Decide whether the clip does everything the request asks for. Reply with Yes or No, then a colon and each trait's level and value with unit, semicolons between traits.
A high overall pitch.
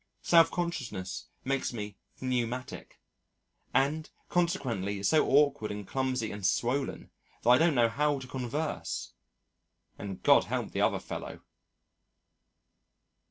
No: low, 130 Hz